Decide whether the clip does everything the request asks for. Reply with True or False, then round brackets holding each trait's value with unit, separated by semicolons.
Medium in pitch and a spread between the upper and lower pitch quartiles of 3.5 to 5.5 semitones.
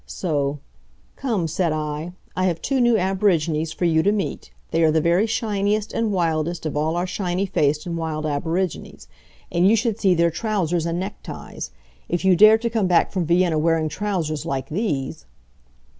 True (175 Hz; 4.0 semitones)